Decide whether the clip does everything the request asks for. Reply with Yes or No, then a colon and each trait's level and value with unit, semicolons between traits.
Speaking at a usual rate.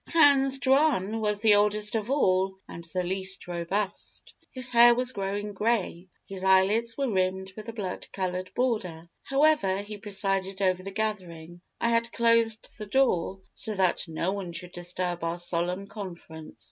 Yes: average, 160 wpm